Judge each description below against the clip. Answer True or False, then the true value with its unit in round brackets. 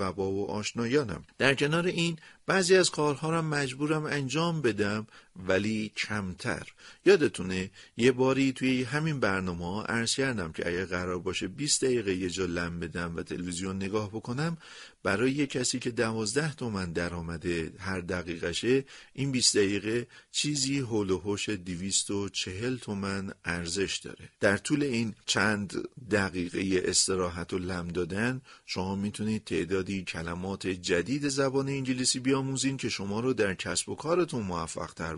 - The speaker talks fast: False (145 wpm)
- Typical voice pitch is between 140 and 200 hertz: False (105 Hz)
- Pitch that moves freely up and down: True (6.3 semitones)